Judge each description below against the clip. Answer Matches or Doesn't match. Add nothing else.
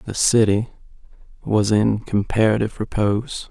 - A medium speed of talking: Doesn't match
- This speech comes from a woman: Doesn't match